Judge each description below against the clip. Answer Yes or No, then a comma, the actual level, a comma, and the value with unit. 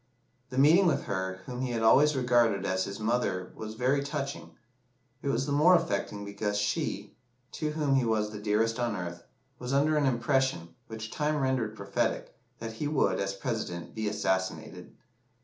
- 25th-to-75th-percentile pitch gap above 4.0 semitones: Yes, average, 5.0 semitones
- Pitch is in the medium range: No, low, 115 Hz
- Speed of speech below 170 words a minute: No, average, 175 wpm